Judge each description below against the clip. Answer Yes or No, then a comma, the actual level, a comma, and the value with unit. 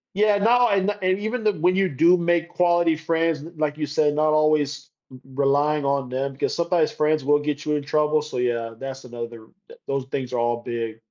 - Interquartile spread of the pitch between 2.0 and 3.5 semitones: No, average, 4.1 semitones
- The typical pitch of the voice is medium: Yes, medium, 150 Hz